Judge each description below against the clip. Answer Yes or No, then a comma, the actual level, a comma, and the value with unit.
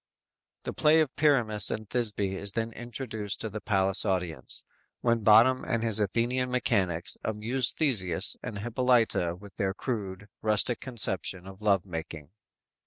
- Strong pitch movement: No, average, 3.8 semitones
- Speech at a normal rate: Yes, average, 150 wpm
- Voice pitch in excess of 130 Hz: No, low, 110 Hz